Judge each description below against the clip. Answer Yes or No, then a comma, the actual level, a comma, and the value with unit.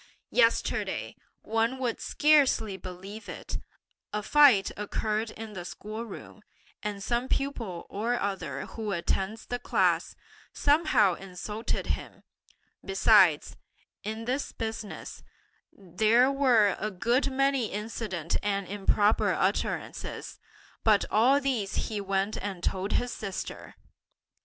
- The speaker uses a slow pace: Yes, slow, 115 wpm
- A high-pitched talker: Yes, high, 215 Hz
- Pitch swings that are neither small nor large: Yes, average, 3.6 semitones